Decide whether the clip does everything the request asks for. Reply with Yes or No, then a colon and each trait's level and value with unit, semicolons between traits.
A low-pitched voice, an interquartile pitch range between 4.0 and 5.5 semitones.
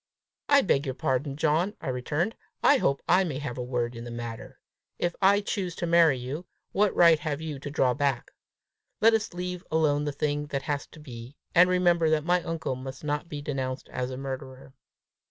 No: medium, 145 Hz; average, 4.7 semitones